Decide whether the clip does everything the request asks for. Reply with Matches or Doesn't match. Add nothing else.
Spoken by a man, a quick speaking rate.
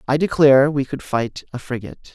Doesn't match